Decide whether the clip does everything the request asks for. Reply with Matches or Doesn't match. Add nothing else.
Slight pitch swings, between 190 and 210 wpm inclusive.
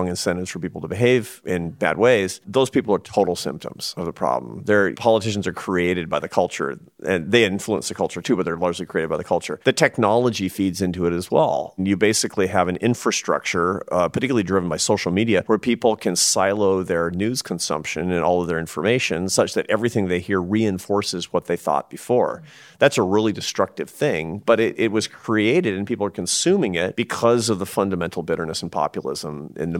Doesn't match